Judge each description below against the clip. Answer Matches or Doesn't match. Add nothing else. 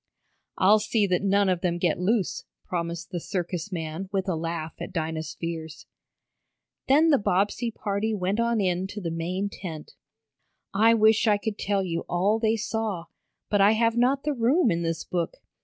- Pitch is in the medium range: Doesn't match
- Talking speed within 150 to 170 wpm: Doesn't match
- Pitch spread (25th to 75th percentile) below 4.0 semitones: Doesn't match